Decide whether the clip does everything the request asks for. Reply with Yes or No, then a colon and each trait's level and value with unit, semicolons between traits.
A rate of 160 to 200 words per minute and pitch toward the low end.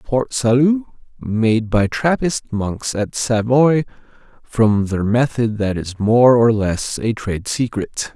No: average, 140 wpm; low, 115 Hz